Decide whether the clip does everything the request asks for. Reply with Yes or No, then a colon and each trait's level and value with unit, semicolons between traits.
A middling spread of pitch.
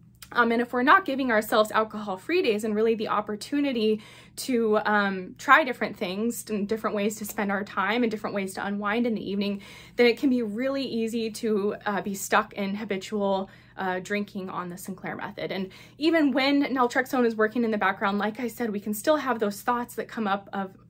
Yes: average, 3.0 semitones